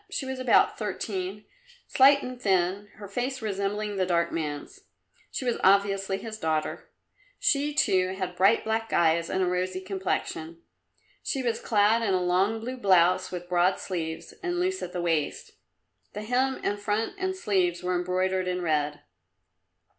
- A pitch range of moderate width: Yes, average, 4.0 semitones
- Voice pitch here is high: Yes, high, 195 Hz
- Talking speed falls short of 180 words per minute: Yes, average, 160 wpm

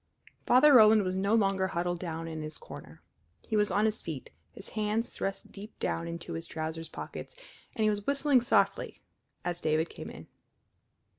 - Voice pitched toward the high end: Yes, high, 195 Hz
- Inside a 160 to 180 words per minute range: Yes, average, 175 wpm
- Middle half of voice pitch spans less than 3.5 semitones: No, average, 4.5 semitones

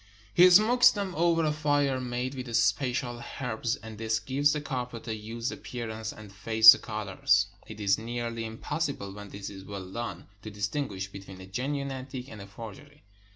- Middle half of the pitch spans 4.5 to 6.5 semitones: Yes, average, 4.8 semitones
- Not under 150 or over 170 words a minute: No, average, 185 wpm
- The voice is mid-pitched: No, low, 115 Hz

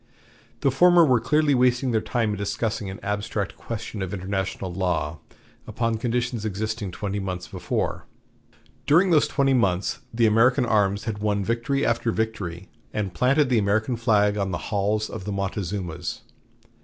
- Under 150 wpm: No, average, 155 wpm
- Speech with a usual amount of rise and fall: Yes, average, 3.5 semitones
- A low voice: Yes, low, 110 Hz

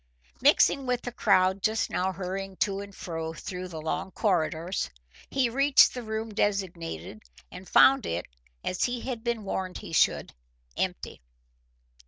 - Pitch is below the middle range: No, high, 195 Hz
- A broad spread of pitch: No, average, 4.1 semitones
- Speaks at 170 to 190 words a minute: No, average, 150 wpm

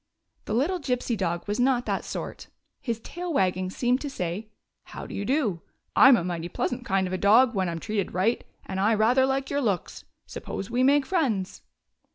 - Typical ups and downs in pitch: No, wide, 5.8 semitones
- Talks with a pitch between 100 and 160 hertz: No, high, 225 Hz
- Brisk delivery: Yes, fast, 215 wpm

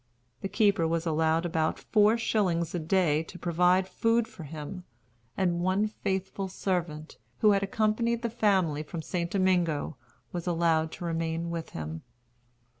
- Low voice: No, medium, 175 Hz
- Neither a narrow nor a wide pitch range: Yes, average, 3.3 semitones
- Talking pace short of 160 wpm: Yes, average, 150 wpm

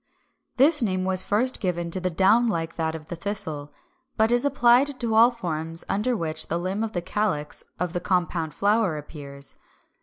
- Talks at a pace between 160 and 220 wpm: Yes, average, 185 wpm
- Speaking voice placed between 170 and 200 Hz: Yes, medium, 185 Hz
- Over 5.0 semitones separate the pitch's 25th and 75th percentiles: Yes, wide, 5.5 semitones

